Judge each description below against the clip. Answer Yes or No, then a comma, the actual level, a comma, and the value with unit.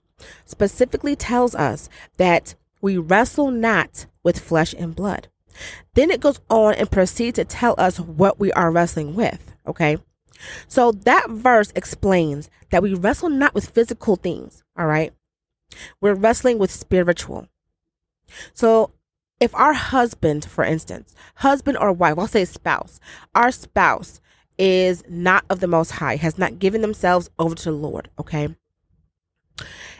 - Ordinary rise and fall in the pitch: No, wide, 5.7 semitones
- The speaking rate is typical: Yes, average, 145 wpm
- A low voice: No, medium, 185 Hz